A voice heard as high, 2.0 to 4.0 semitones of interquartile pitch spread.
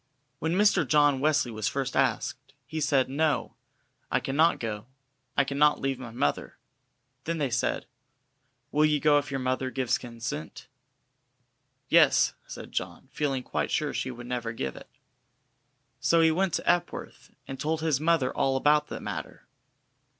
No: low, 135 Hz; average, 3.2 semitones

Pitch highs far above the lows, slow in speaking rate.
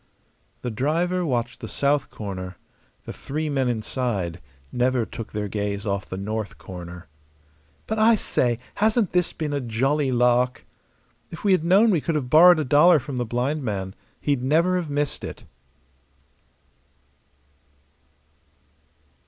No: wide, 6.2 semitones; average, 145 wpm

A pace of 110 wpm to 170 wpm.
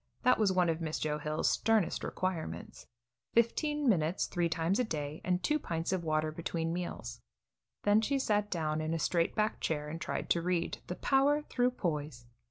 No: average, 185 wpm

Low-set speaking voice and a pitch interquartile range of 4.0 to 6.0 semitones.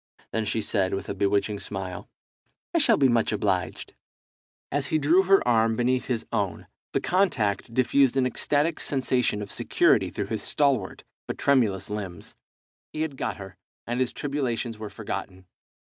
Yes: low, 115 Hz; average, 5.3 semitones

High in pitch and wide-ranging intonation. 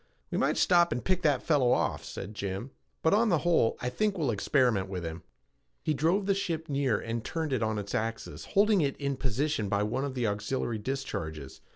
No: low, 130 Hz; wide, 7.0 semitones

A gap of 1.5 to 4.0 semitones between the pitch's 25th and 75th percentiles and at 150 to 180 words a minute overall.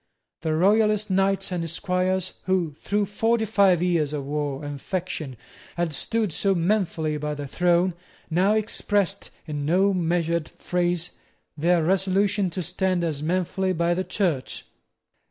No: average, 3.2 semitones; average, 140 wpm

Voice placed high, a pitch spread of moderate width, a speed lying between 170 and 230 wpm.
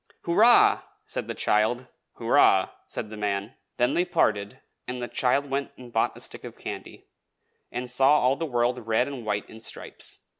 No: low, 125 Hz; average, 3.6 semitones; average, 180 wpm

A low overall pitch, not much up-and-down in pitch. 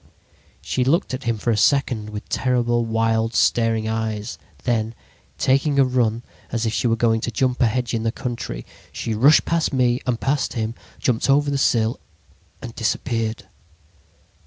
Yes: low, 115 Hz; narrow, 2.3 semitones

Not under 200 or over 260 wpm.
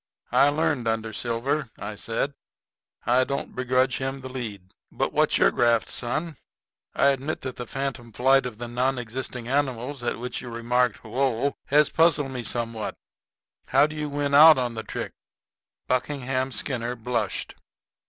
No: average, 160 wpm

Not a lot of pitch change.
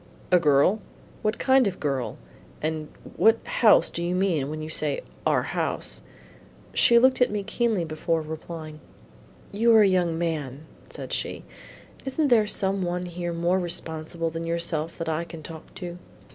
No: average, 3.9 semitones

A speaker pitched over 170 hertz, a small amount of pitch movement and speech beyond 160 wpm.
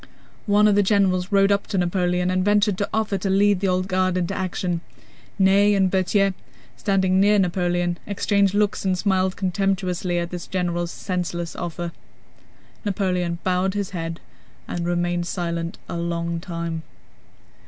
No: medium, 185 Hz; narrow, 2.1 semitones; average, 155 wpm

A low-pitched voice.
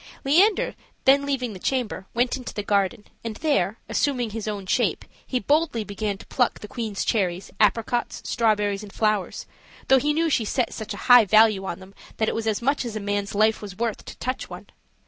No: high, 220 Hz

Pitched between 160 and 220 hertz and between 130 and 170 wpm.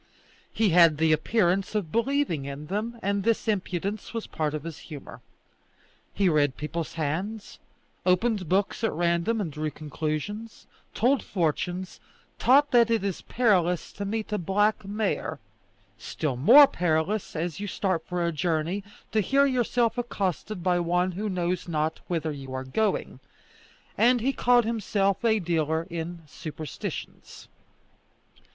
Yes: medium, 185 Hz; average, 145 wpm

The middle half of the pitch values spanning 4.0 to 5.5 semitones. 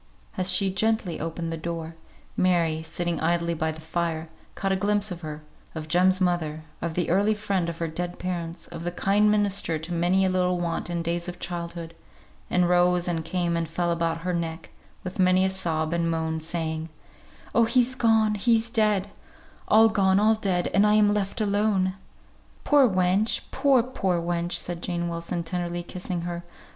No: average, 2.7 semitones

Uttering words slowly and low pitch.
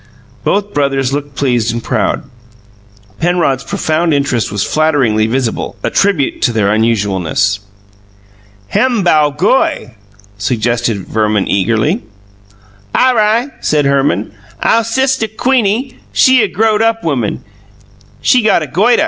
No: slow, 125 wpm; medium, 145 Hz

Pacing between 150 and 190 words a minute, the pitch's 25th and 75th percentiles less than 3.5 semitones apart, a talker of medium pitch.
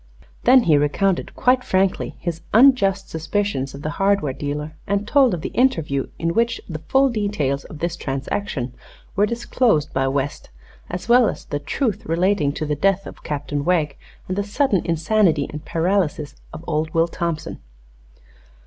No: average, 165 wpm; wide, 5.5 semitones; medium, 170 Hz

